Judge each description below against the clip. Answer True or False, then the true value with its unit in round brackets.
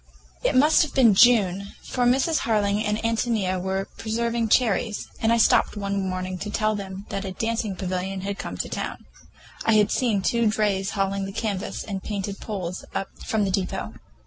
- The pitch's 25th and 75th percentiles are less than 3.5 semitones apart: True (2.8 semitones)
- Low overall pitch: False (205 Hz)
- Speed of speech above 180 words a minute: True (190 wpm)